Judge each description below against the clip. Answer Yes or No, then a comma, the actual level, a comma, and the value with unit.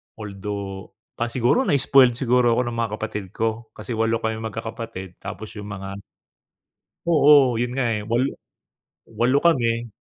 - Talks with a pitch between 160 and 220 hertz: No, low, 115 Hz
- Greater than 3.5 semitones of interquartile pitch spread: No, average, 2.7 semitones